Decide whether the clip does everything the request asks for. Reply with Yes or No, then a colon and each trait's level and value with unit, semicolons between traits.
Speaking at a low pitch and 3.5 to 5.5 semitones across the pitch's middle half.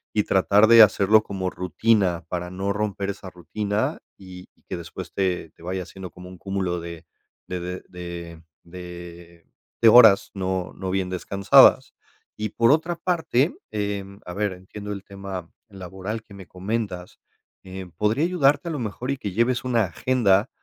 No: very low, 95 Hz; average, 3.0 semitones